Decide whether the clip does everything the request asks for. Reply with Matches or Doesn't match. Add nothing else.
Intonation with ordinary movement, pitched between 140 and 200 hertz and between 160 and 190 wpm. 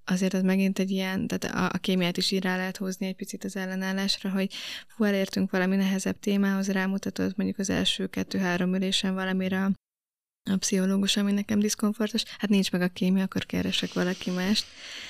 Doesn't match